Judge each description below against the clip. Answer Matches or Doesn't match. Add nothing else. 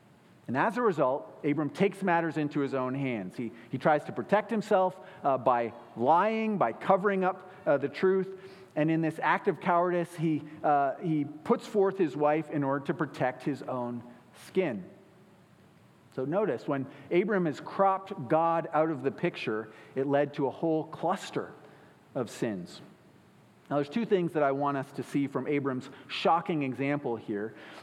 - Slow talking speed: Doesn't match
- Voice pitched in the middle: Matches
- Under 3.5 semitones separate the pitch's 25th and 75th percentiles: Doesn't match